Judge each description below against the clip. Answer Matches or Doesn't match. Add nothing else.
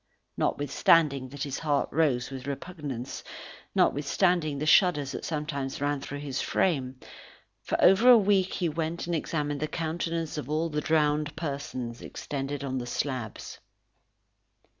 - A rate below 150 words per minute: Matches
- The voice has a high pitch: Doesn't match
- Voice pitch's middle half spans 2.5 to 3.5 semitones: Matches